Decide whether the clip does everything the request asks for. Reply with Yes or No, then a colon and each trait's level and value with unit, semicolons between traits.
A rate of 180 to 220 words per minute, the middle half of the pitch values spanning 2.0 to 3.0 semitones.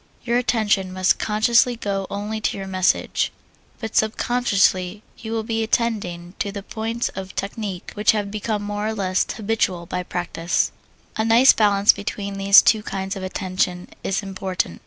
No: average, 160 wpm; average, 2.7 semitones